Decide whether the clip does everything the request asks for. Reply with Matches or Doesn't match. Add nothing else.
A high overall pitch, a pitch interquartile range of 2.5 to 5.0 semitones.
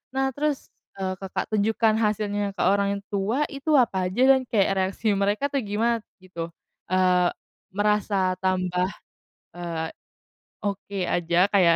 Matches